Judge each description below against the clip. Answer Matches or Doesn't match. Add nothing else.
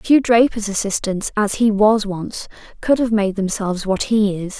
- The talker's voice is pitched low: Doesn't match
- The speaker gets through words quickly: Doesn't match